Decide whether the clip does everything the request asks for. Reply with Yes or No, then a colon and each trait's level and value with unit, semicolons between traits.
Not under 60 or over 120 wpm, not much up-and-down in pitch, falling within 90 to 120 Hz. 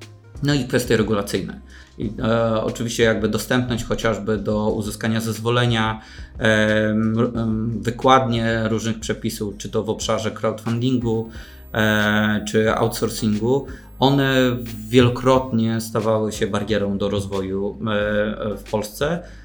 Yes: slow, 110 wpm; narrow, 1.4 semitones; low, 110 Hz